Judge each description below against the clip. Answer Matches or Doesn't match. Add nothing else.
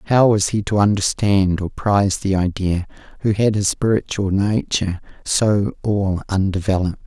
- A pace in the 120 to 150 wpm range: Matches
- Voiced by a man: Matches